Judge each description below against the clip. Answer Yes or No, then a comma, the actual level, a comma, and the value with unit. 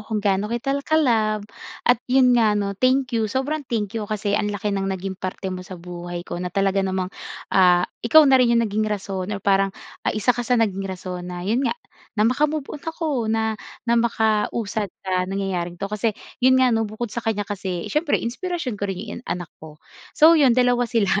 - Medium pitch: No, high, 215 Hz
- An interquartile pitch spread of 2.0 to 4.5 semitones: Yes, average, 4.0 semitones